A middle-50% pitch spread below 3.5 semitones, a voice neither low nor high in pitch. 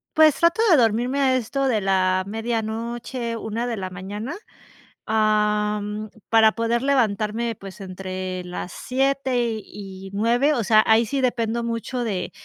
No: average, 2.9 semitones; high, 225 Hz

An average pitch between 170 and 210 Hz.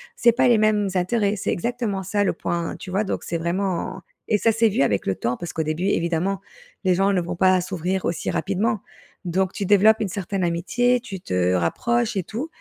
Yes: high, 190 Hz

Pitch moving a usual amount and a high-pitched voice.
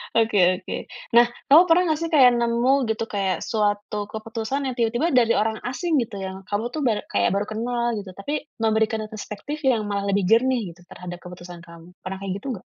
Yes: average, 3.4 semitones; high, 220 Hz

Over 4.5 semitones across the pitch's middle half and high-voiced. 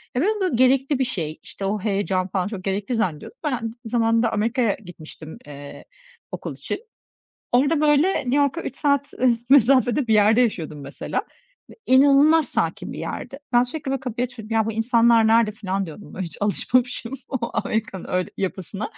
Yes: average, 5.1 semitones; high, 230 Hz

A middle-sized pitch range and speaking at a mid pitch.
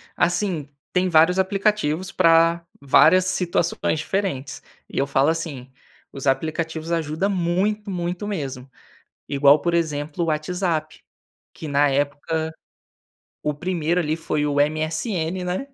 Yes: average, 3.4 semitones; medium, 165 Hz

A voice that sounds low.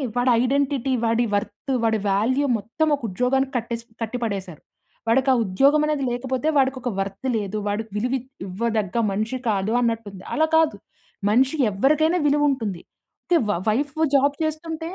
No: high, 245 Hz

